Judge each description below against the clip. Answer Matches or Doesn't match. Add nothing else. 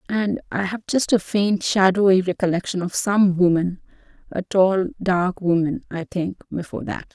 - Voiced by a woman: Matches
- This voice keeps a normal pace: Matches